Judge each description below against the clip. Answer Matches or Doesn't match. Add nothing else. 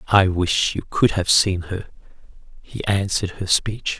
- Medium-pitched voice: Doesn't match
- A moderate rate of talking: Matches